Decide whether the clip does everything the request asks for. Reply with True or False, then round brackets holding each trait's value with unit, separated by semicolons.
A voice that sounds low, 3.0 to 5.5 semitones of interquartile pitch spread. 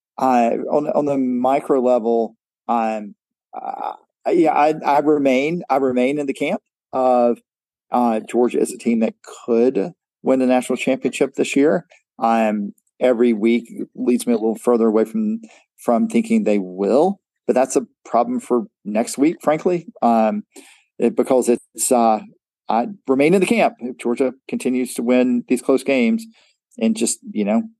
True (125 Hz; 3.7 semitones)